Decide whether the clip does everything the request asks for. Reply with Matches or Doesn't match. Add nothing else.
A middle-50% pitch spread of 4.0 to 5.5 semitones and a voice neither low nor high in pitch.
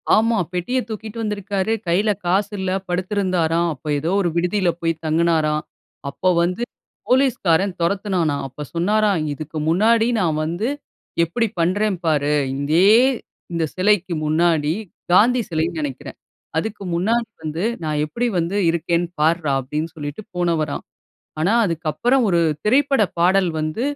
Matches